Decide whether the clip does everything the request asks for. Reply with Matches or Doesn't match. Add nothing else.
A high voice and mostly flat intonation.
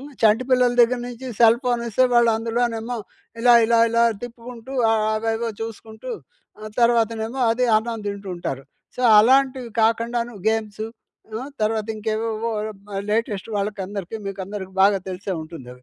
Matches